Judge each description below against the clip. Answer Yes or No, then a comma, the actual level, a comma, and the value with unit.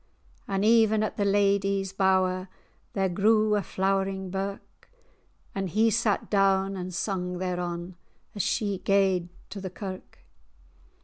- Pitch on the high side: Yes, high, 195 Hz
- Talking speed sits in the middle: No, slow, 130 wpm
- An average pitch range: No, narrow, 1.4 semitones